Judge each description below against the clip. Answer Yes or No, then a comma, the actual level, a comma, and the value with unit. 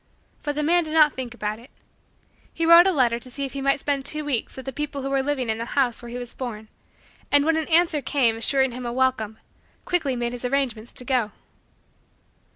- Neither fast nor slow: No, fast, 230 wpm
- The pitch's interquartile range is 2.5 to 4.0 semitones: Yes, average, 3.4 semitones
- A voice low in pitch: No, very high, 265 Hz